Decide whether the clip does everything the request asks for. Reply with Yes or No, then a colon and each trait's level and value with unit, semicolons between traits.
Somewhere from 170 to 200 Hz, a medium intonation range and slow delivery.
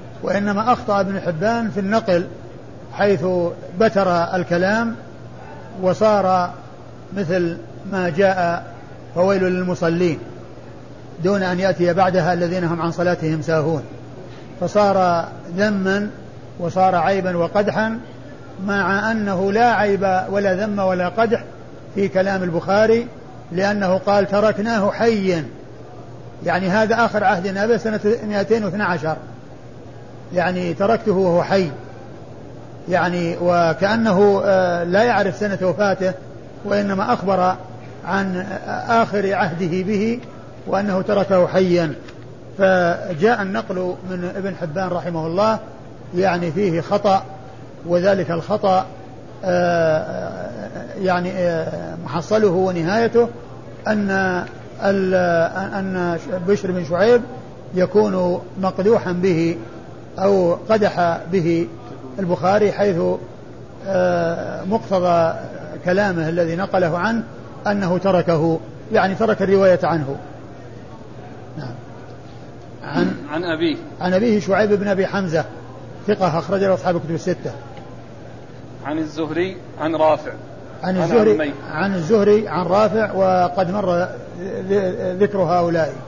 No: medium, 185 Hz; average, 3.3 semitones; average, 95 wpm